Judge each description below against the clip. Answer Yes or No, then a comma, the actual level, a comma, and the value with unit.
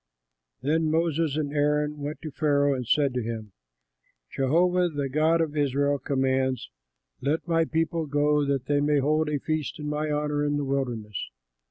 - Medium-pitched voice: Yes, medium, 145 Hz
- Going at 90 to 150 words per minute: No, average, 170 wpm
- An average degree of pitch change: No, narrow, 2.0 semitones